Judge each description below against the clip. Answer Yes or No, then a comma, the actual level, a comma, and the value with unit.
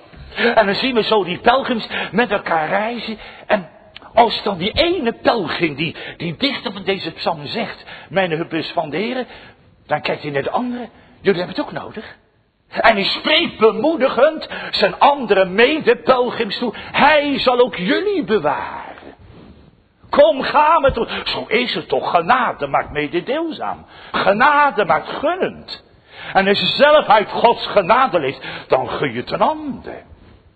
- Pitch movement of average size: No, wide, 7.4 semitones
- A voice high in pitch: Yes, high, 225 Hz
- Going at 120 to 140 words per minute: No, average, 155 wpm